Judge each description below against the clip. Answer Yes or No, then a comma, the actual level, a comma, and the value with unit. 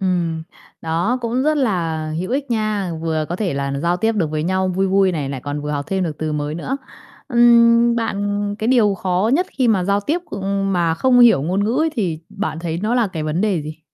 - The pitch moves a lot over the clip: Yes, wide, 5.7 semitones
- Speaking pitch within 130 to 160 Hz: No, high, 190 Hz